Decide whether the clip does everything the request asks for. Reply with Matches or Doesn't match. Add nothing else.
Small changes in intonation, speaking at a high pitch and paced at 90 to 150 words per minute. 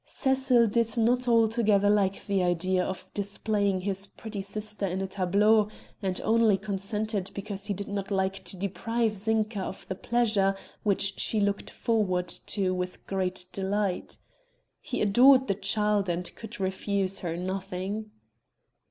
Matches